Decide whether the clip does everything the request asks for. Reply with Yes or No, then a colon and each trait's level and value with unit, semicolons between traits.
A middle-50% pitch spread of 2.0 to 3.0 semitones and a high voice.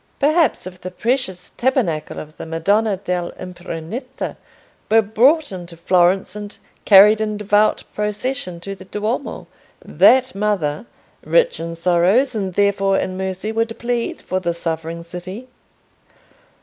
No: average, 4.1 semitones; high, 195 Hz